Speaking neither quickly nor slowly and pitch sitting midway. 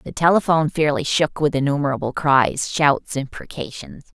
No: slow, 130 wpm; medium, 145 Hz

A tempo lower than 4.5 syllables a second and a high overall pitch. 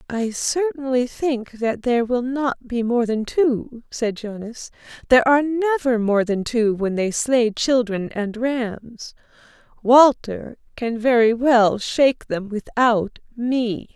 Yes: 3.7 syllables/s; high, 240 Hz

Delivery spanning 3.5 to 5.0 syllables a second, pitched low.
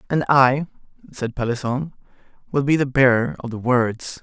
Yes: 4.8 syllables/s; low, 130 Hz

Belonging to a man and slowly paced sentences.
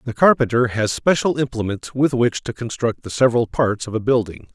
No: male; average, 200 wpm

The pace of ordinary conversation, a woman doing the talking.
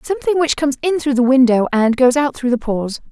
No: fast, 250 wpm; female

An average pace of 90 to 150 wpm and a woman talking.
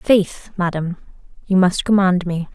Yes: average, 140 wpm; female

